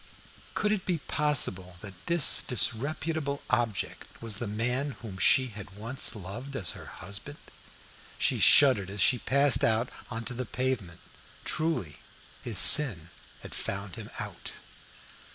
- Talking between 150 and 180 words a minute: No, average, 140 wpm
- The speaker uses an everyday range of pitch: No, wide, 5.8 semitones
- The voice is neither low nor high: No, low, 120 Hz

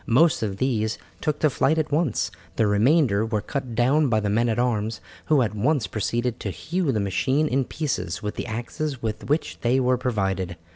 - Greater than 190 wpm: Yes, average, 200 wpm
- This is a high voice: No, low, 120 Hz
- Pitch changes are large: No, average, 4.7 semitones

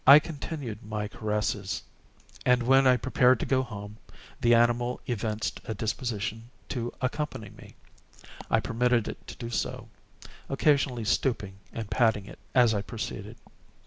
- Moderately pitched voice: No, low, 120 Hz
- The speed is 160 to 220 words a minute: No, average, 145 wpm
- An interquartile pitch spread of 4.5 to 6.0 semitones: No, average, 3.1 semitones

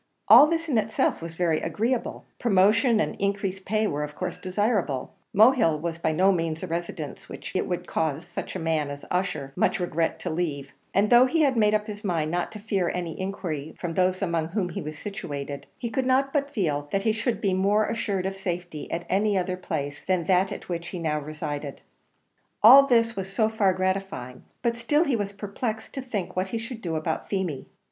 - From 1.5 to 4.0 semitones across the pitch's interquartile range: No, average, 4.9 semitones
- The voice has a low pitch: No, high, 190 Hz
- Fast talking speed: Yes, fast, 210 wpm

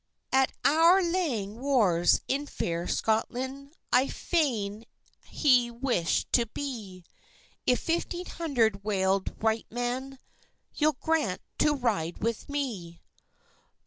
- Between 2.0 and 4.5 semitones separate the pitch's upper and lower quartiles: No, wide, 5.6 semitones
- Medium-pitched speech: No, high, 245 Hz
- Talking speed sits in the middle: No, slow, 110 wpm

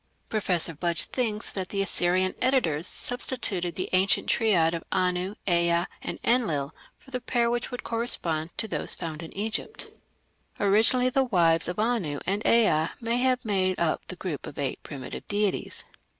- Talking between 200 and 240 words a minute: No, average, 165 wpm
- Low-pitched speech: No, high, 190 Hz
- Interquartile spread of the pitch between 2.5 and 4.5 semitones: No, wide, 5.4 semitones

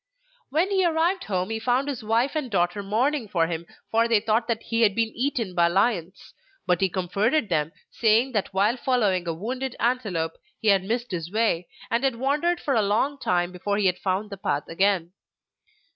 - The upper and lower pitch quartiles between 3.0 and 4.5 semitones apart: No, average, 5.2 semitones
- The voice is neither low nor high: No, high, 215 Hz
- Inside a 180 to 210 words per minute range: Yes, average, 200 wpm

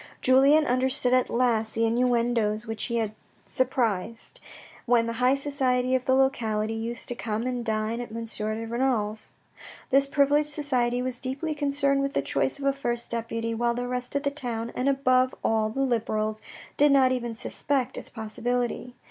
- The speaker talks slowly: No, average, 175 wpm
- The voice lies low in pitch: No, high, 245 Hz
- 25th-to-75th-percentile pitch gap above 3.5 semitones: No, average, 2.7 semitones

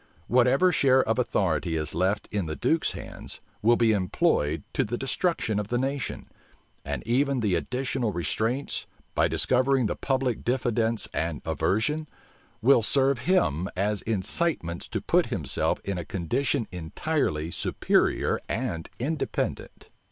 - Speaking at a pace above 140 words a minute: No, slow, 135 wpm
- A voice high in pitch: No, low, 115 Hz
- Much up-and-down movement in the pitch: Yes, wide, 6.4 semitones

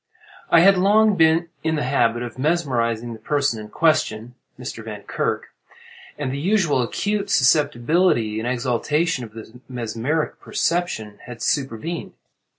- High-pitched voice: No, low, 130 Hz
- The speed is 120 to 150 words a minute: Yes, slow, 135 wpm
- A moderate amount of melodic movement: No, wide, 6.1 semitones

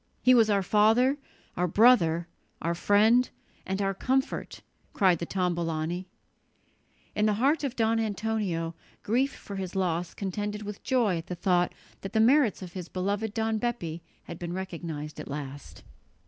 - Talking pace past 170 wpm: No, average, 160 wpm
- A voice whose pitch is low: No, high, 195 Hz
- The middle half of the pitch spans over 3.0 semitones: Yes, average, 4.4 semitones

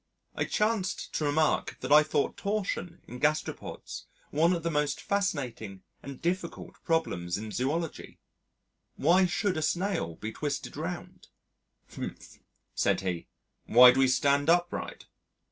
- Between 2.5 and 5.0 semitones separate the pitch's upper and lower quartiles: No, wide, 5.5 semitones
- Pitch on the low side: No, medium, 155 Hz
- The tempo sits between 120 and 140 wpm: Yes, slow, 135 wpm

